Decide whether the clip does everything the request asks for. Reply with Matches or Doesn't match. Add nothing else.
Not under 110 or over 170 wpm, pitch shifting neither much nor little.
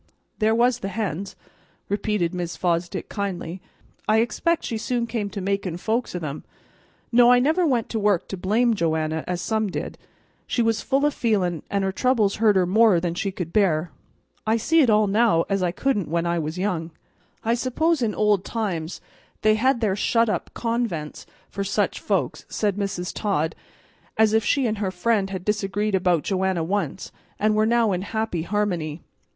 Doesn't match